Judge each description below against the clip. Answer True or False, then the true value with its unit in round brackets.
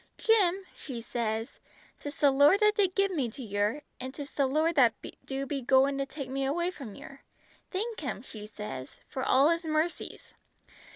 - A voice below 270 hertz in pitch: False (275 Hz)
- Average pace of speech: True (185 wpm)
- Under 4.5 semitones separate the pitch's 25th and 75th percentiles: False (4.8 semitones)